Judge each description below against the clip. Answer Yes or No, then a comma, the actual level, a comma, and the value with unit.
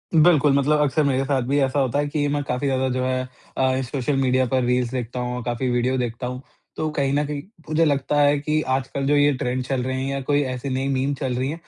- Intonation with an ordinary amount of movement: No, narrow, 2.1 semitones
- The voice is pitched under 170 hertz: Yes, low, 135 Hz